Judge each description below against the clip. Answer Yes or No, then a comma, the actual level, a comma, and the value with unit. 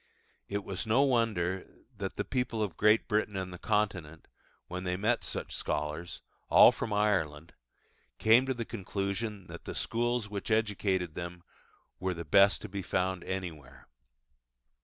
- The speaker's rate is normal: Yes, average, 155 wpm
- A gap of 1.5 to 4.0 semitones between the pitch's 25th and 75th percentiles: Yes, average, 3.4 semitones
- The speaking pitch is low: Yes, low, 100 Hz